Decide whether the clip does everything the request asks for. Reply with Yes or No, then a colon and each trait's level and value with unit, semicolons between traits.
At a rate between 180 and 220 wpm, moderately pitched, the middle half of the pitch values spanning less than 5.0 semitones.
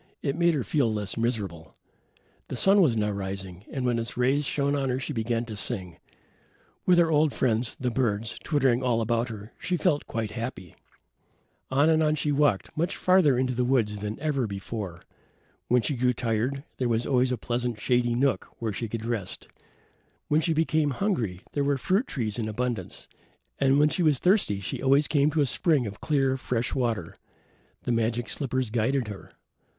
No: average, 190 wpm; low, 125 Hz; average, 4.2 semitones